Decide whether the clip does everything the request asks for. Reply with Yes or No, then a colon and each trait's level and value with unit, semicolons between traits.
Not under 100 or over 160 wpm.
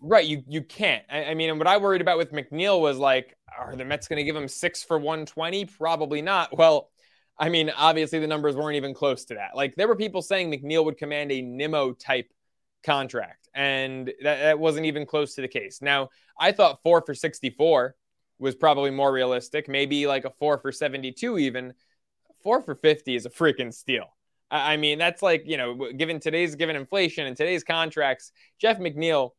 No: fast, 205 wpm